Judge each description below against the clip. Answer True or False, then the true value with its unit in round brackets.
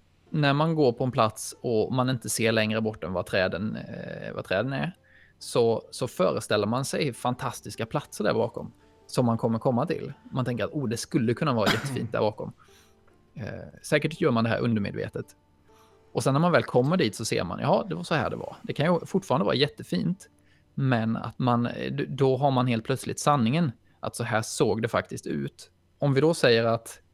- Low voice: True (120 Hz)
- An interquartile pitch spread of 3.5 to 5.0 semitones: True (4.4 semitones)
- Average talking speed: False (210 wpm)